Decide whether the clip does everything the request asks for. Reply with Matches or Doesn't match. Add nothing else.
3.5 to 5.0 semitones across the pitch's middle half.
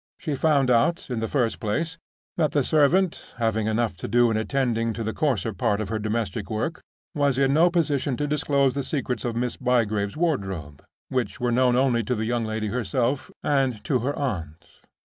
Matches